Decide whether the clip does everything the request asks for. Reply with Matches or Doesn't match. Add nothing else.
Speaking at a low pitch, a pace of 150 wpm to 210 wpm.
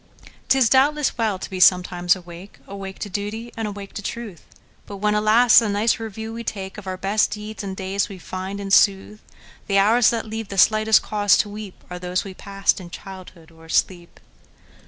Doesn't match